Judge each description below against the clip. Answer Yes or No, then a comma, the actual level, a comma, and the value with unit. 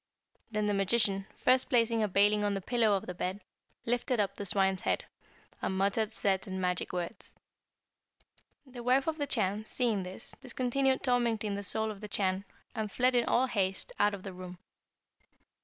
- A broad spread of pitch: No, average, 3.7 semitones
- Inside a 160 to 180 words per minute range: Yes, average, 175 wpm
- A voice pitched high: Yes, high, 210 Hz